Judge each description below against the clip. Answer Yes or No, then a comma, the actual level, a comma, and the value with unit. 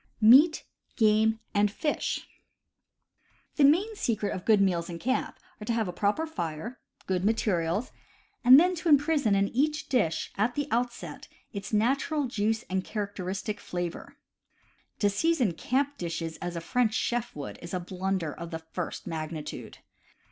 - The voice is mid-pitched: No, high, 210 Hz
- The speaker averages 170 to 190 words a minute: No, average, 155 wpm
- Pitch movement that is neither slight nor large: No, wide, 6.3 semitones